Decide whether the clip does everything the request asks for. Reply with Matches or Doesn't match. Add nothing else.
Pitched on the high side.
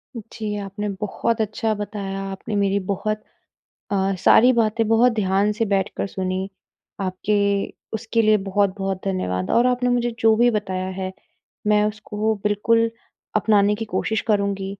Matches